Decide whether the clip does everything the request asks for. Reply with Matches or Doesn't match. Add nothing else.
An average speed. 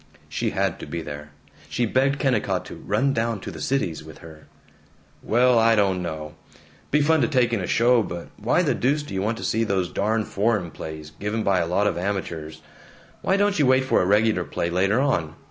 Doesn't match